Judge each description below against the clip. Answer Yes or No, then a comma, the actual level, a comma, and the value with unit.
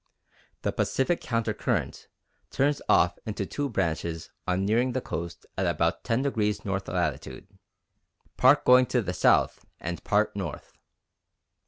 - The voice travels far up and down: Yes, wide, 5.8 semitones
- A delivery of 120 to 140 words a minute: Yes, slow, 135 wpm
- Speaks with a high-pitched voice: No, low, 105 Hz